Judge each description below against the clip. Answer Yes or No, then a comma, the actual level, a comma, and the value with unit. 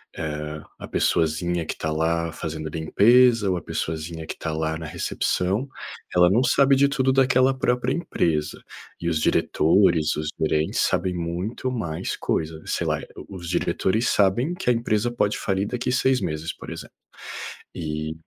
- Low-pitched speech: Yes, very low, 90 Hz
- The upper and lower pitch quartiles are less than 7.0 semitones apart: No, wide, 7.3 semitones